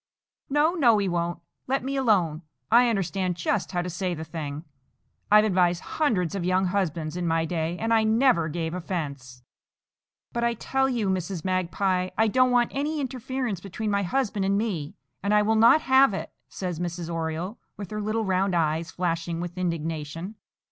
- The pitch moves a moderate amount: Yes, average, 4.7 semitones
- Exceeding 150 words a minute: Yes, average, 180 wpm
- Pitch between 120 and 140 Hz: No, medium, 185 Hz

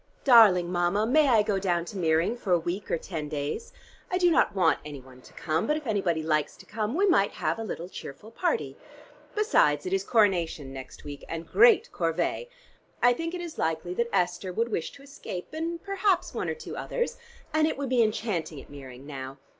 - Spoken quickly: Yes, fast, 210 wpm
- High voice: Yes, high, 195 Hz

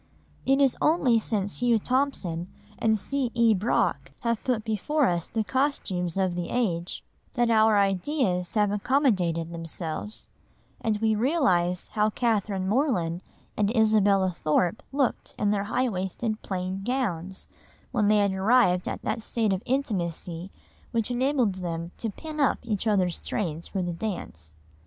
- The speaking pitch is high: Yes, high, 210 Hz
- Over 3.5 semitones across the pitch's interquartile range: Yes, average, 4.8 semitones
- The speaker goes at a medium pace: Yes, average, 150 wpm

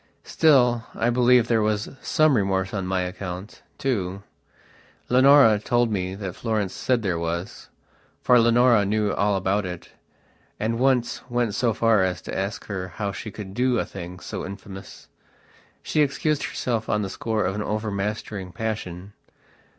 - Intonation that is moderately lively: Yes, average, 3.9 semitones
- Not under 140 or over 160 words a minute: Yes, average, 155 wpm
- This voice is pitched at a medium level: No, low, 105 Hz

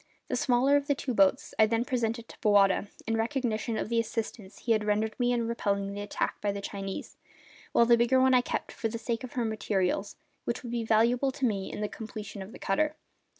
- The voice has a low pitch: No, high, 225 Hz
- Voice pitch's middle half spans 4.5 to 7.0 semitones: No, average, 2.7 semitones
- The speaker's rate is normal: No, fast, 230 wpm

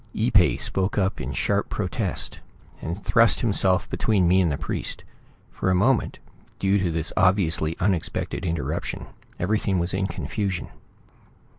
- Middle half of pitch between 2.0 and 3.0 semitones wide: Yes, average, 2.7 semitones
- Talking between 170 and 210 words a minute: No, average, 145 wpm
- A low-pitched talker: Yes, very low, 95 Hz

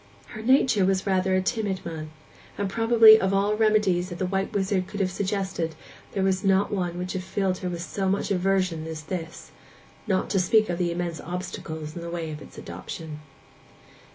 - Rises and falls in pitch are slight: Yes, narrow, 2.3 semitones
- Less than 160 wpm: No, average, 200 wpm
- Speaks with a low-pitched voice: No, medium, 185 Hz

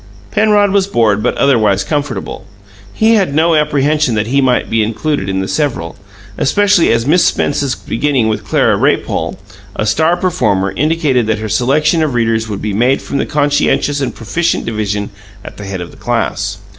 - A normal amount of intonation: No, wide, 6.1 semitones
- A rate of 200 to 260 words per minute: No, average, 180 wpm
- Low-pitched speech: Yes, low, 130 Hz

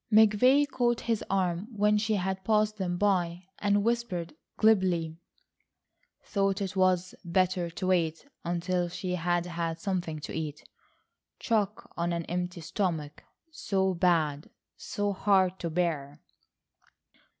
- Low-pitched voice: No, medium, 185 Hz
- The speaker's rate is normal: No, slow, 120 wpm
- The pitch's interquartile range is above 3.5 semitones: No, average, 3.1 semitones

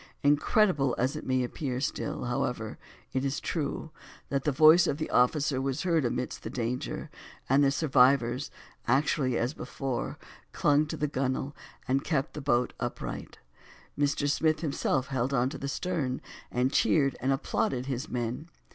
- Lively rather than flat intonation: No, average, 2.7 semitones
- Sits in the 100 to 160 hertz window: Yes, low, 135 Hz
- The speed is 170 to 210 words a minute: No, average, 160 wpm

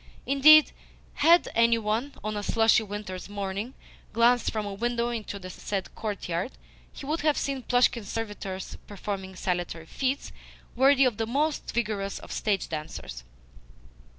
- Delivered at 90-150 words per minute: Yes, average, 145 wpm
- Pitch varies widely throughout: No, average, 4.1 semitones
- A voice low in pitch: No, high, 220 Hz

